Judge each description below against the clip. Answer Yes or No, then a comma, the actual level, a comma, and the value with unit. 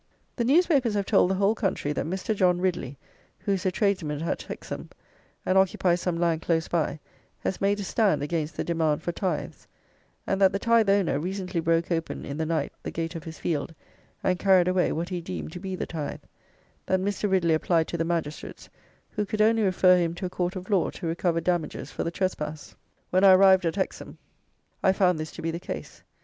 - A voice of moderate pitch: Yes, medium, 180 Hz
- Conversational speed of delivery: No, fast, 215 wpm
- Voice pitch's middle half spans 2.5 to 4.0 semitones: Yes, average, 2.8 semitones